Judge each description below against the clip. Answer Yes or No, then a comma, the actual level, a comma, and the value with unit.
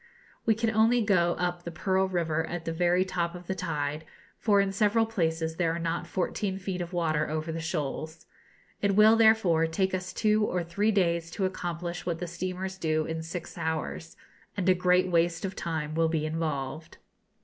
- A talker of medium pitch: Yes, medium, 175 Hz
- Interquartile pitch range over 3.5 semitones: No, narrow, 2.6 semitones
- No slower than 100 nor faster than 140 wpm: No, average, 195 wpm